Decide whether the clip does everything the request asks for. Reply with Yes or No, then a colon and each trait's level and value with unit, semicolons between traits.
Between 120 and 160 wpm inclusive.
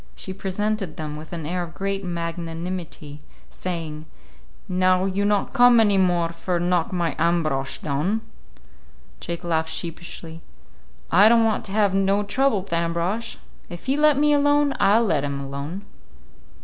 Yes: average, 150 wpm